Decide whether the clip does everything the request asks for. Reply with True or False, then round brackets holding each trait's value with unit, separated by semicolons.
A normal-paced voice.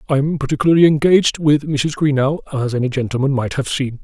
True (180 wpm)